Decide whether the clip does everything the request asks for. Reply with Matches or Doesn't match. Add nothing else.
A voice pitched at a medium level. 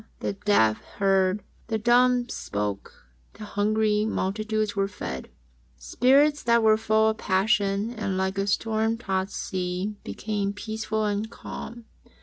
Doesn't match